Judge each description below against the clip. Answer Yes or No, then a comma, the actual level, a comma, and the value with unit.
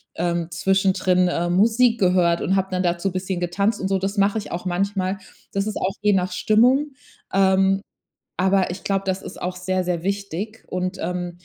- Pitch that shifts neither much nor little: No, narrow, 1.7 semitones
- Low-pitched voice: No, high, 190 Hz